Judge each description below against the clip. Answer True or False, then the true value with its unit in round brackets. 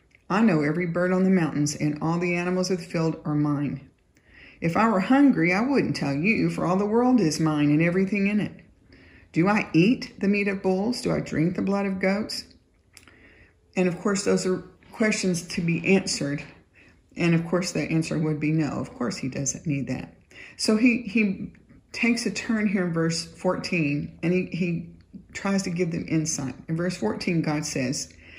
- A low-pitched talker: False (180 Hz)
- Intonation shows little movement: False (4.7 semitones)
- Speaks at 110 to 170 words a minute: False (200 wpm)